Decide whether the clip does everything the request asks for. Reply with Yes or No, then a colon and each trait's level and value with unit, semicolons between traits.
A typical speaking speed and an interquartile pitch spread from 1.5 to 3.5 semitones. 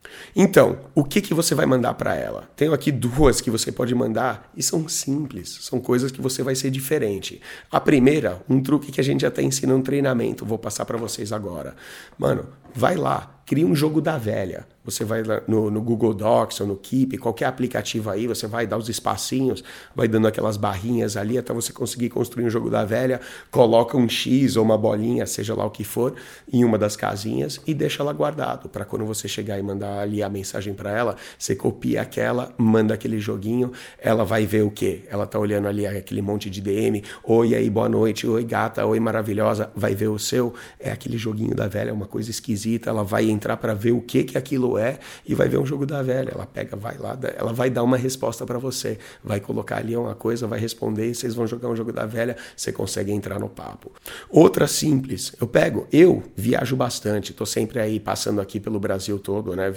No: fast, 220 wpm; average, 3.1 semitones